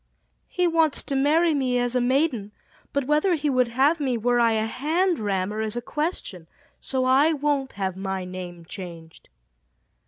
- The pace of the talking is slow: No, average, 175 wpm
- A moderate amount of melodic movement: No, wide, 6.3 semitones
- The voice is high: Yes, very high, 255 Hz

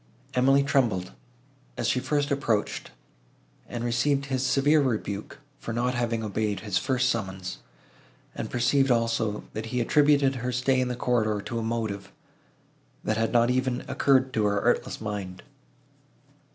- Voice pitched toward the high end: No, low, 120 Hz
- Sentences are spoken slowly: No, average, 145 wpm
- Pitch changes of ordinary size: Yes, average, 3.3 semitones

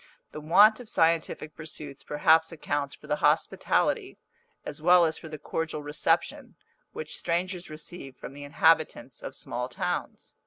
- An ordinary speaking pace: Yes, average, 150 wpm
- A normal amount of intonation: No, narrow, 2.1 semitones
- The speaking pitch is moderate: Yes, medium, 160 Hz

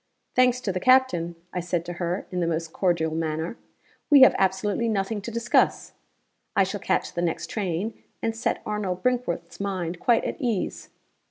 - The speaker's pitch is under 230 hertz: Yes, high, 190 Hz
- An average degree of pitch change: Yes, average, 4.8 semitones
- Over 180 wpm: No, average, 175 wpm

